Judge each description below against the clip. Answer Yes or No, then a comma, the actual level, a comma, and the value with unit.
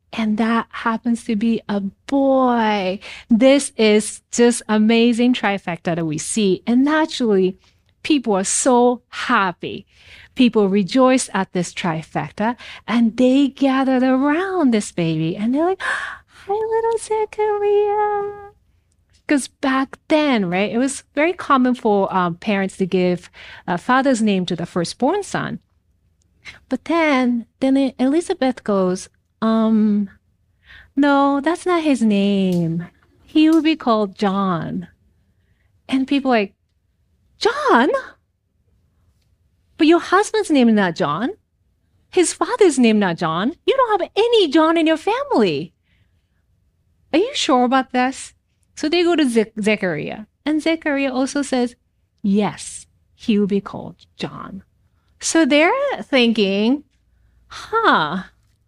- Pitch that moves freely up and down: Yes, wide, 7.1 semitones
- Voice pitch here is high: Yes, high, 240 Hz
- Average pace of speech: No, slow, 130 wpm